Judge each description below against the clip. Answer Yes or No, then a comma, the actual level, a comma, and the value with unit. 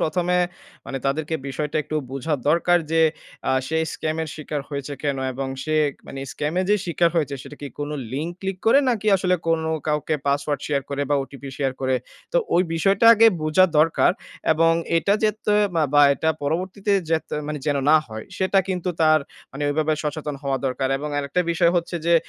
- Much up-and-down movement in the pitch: No, average, 3.2 semitones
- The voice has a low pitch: No, medium, 155 Hz